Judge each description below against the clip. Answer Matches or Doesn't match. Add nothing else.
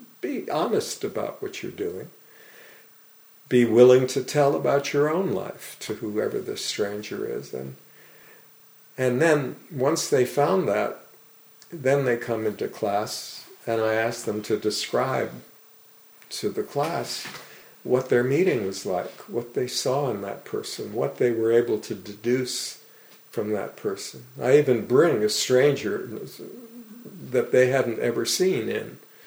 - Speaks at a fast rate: Doesn't match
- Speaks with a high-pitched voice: Doesn't match